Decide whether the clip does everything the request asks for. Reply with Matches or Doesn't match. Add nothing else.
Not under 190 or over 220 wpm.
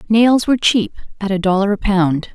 Matches